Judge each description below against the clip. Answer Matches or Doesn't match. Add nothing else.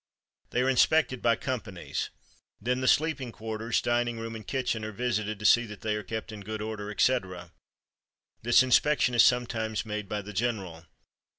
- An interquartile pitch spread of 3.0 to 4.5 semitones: Doesn't match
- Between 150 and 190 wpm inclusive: Matches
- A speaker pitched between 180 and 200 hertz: Doesn't match